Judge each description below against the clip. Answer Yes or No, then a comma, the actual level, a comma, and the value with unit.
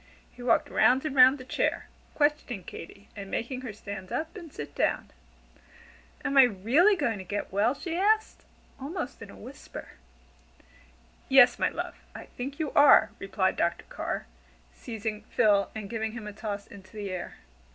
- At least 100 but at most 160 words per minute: No, average, 170 wpm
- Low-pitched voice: No, high, 235 Hz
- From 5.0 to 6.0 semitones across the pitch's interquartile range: Yes, wide, 5.6 semitones